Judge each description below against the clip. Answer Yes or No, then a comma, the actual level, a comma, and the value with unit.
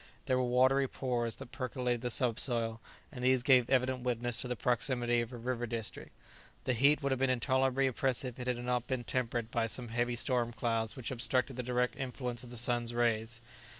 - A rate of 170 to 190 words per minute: No, fast, 205 wpm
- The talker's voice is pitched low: Yes, low, 125 Hz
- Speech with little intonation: Yes, narrow, 1.4 semitones